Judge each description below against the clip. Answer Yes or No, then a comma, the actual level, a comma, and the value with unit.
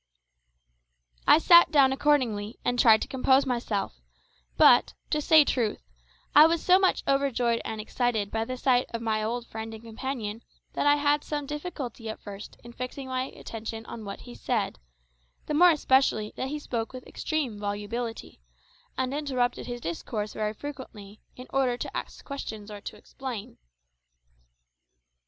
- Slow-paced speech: No, average, 160 wpm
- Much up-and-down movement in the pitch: No, average, 4.1 semitones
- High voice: Yes, high, 245 Hz